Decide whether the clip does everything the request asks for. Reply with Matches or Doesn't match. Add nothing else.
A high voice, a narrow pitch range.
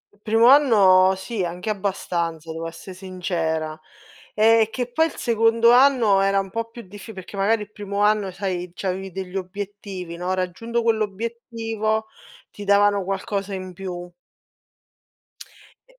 Doesn't match